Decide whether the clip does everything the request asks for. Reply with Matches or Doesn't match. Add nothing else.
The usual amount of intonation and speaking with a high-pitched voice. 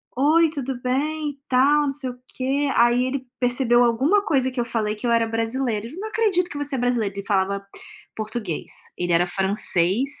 Matches